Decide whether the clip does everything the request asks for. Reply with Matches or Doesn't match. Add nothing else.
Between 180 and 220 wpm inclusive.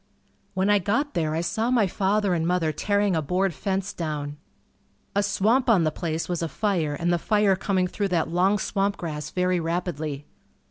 Matches